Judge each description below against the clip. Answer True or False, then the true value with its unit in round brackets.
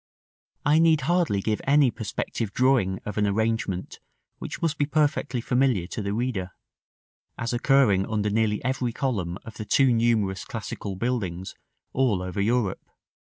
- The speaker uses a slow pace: False (155 wpm)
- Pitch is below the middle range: True (115 Hz)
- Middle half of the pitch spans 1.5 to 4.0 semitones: False (4.7 semitones)